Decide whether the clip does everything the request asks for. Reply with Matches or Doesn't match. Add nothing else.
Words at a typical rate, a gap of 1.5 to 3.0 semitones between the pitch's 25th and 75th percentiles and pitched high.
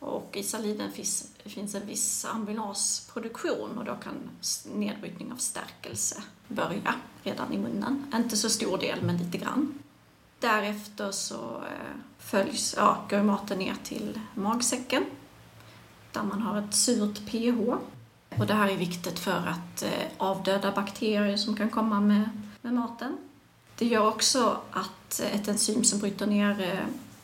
Matches